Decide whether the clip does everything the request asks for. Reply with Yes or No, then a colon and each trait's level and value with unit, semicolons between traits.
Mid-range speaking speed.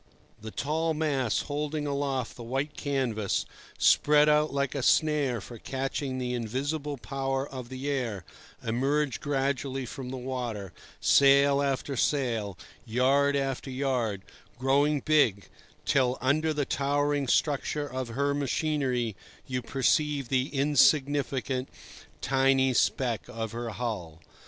No: slow, 125 wpm